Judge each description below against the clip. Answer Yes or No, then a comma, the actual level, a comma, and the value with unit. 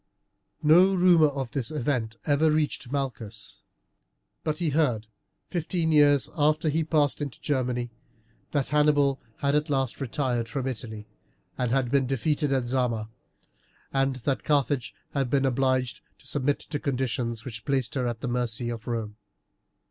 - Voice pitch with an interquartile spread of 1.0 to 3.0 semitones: No, average, 3.4 semitones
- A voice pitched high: No, low, 135 Hz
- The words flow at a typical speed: Yes, average, 155 wpm